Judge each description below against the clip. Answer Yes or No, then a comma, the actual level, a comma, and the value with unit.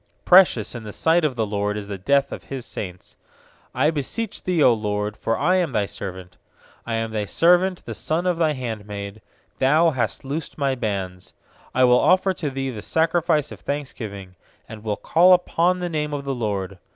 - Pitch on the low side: Yes, low, 130 Hz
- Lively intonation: Yes, wide, 7.6 semitones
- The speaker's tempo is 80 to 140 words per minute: No, average, 195 wpm